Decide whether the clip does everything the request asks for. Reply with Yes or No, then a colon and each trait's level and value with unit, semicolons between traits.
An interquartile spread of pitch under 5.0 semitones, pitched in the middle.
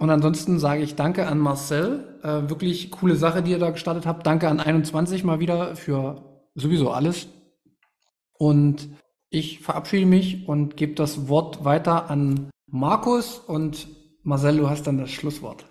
Yes: narrow, 2.5 semitones; medium, 155 Hz